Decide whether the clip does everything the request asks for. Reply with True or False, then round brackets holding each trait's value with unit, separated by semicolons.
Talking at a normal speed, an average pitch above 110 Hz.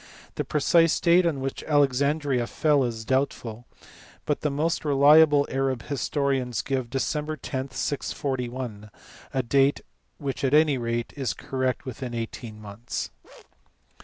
False (130 wpm; 135 Hz)